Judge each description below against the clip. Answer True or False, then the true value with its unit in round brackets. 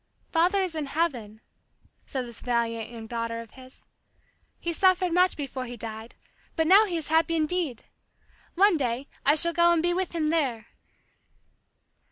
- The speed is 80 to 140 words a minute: False (165 wpm)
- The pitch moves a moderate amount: False (6.4 semitones)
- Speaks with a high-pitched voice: True (305 Hz)